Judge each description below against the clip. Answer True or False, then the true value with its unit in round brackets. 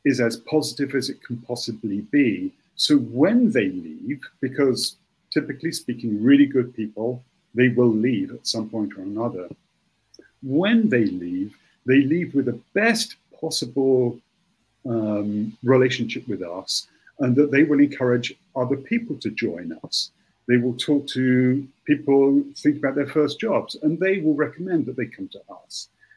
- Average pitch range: True (5.0 semitones)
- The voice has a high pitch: False (140 Hz)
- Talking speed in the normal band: True (155 wpm)